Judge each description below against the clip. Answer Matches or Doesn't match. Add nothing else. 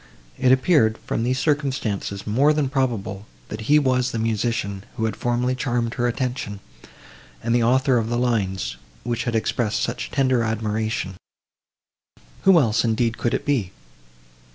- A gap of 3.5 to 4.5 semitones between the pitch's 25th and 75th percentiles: Doesn't match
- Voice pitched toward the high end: Doesn't match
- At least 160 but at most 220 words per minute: Doesn't match